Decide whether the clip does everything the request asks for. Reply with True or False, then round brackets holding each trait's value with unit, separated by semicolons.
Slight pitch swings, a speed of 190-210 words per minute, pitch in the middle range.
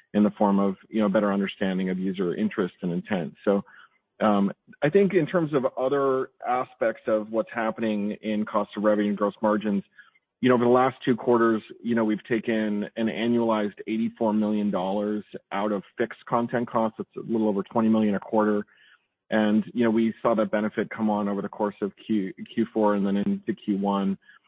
False (2.0 semitones; 195 wpm; 110 Hz)